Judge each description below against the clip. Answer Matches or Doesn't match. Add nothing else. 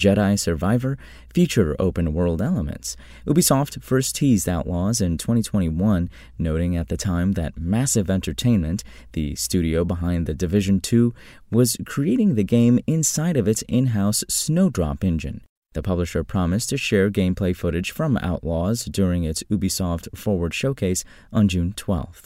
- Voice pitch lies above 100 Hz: Doesn't match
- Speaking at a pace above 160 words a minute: Doesn't match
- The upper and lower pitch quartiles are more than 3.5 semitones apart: Matches